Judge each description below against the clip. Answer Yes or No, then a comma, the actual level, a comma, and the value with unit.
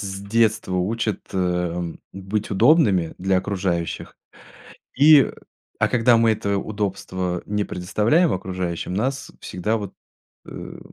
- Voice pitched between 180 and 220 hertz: No, low, 100 Hz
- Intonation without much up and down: No, average, 3.5 semitones